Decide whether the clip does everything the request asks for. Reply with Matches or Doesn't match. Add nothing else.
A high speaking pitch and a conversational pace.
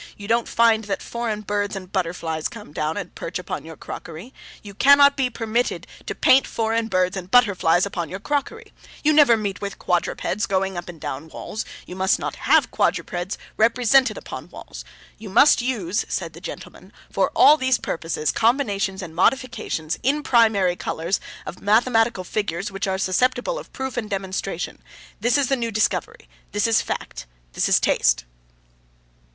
Matches